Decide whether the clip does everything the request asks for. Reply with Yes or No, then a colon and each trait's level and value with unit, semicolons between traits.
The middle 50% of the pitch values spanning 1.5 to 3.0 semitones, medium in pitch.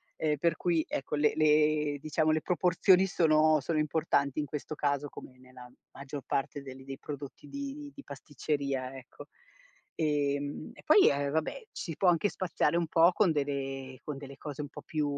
Yes: narrow, 2.5 semitones; medium, 150 Hz